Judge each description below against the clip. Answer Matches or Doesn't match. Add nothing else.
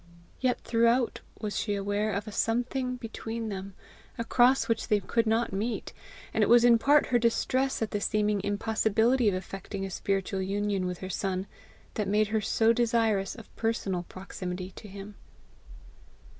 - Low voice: Doesn't match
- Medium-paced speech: Matches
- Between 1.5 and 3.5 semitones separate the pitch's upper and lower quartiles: Matches